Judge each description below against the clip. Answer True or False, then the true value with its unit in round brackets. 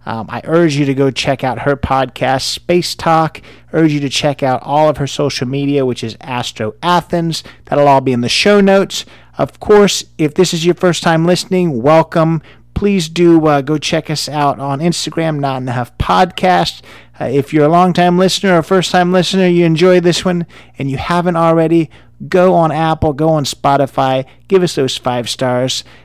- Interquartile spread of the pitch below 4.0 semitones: False (4.5 semitones)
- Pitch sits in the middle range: True (155 Hz)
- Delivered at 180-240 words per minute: True (200 wpm)